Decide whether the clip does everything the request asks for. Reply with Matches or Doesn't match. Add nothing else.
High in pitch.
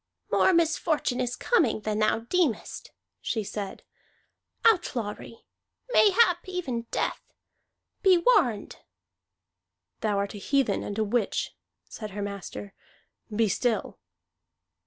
Matches